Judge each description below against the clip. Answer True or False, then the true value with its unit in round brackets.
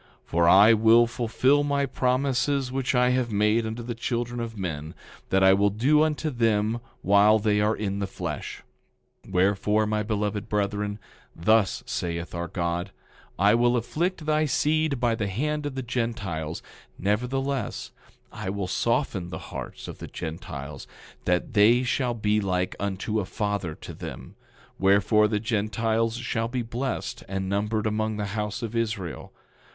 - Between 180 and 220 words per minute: False (160 wpm)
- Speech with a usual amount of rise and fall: True (3.4 semitones)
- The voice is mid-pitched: False (110 Hz)